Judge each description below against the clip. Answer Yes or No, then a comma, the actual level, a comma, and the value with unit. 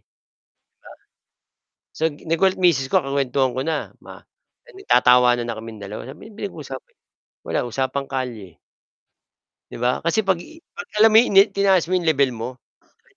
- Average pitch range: No, wide, 7.2 semitones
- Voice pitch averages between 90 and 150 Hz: Yes, medium, 140 Hz